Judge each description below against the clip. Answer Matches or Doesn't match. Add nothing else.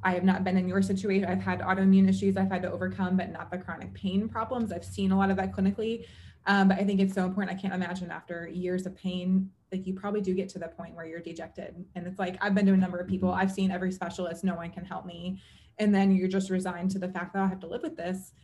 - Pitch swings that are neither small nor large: Doesn't match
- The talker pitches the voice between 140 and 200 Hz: Matches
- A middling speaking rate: Doesn't match